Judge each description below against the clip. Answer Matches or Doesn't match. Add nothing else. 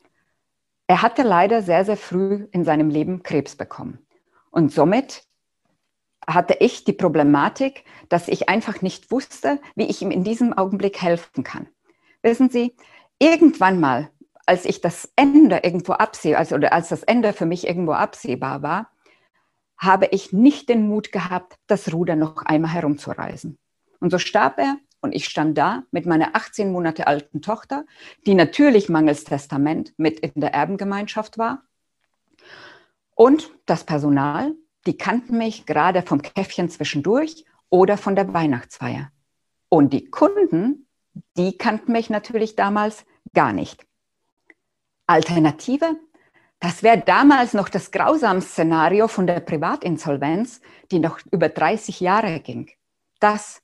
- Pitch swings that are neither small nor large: Doesn't match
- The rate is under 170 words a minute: Matches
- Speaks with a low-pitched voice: Doesn't match